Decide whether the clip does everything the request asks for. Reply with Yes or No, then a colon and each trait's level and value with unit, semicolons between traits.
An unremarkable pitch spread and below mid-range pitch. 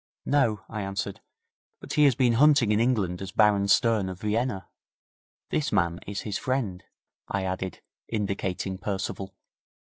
Yes: average, 3.5 semitones; low, 105 Hz